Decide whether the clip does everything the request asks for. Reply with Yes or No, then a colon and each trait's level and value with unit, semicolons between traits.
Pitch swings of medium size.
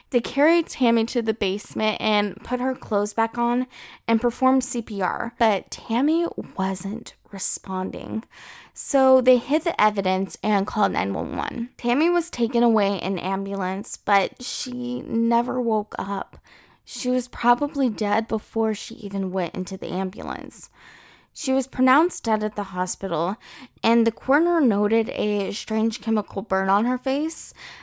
Yes: average, 3.7 semitones